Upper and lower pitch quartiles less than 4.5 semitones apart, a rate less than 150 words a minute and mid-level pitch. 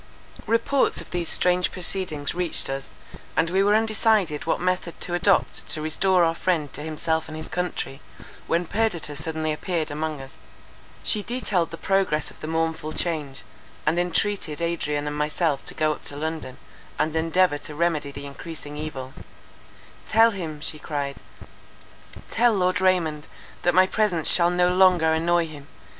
No: average, 3.1 semitones; average, 160 wpm; medium, 165 Hz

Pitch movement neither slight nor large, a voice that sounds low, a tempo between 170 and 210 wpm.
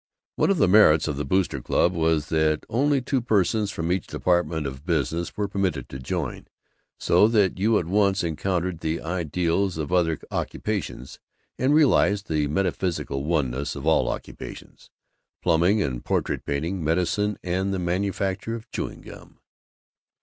No: average, 4.1 semitones; very low, 90 Hz; average, 155 wpm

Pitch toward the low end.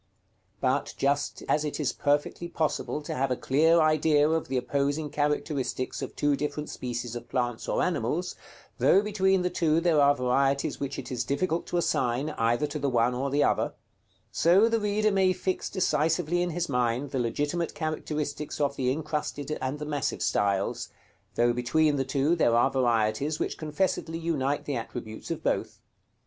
No: medium, 145 Hz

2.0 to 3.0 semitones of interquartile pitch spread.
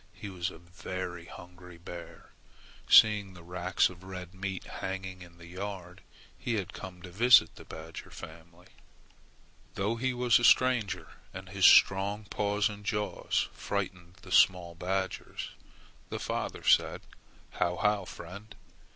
Yes: narrow, 2.6 semitones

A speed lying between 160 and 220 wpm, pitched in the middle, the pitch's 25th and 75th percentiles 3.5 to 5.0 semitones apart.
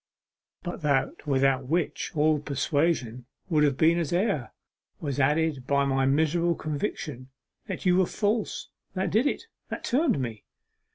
No: average, 150 wpm; medium, 150 Hz; average, 4.3 semitones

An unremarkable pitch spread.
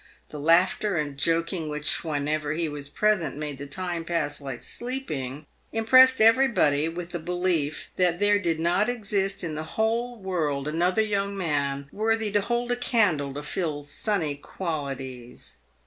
No: wide, 5.8 semitones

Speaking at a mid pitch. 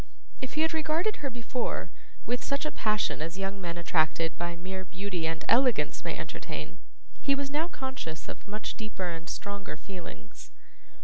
No: high, 200 Hz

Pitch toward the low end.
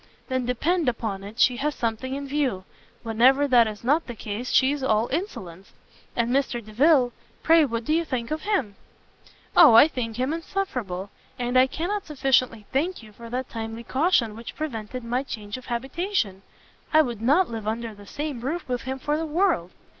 No: very high, 250 Hz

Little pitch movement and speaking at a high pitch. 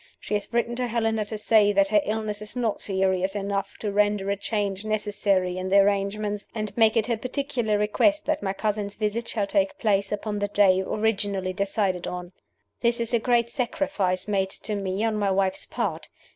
Yes: narrow, 2.1 semitones; high, 210 Hz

